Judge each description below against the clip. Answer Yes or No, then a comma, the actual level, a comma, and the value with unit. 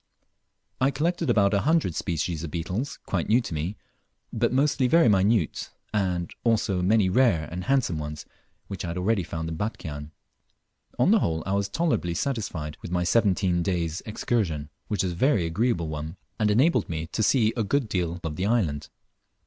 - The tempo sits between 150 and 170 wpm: No, average, 180 wpm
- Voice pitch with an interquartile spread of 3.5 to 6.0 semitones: Yes, wide, 5.5 semitones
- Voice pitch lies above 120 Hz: No, very low, 95 Hz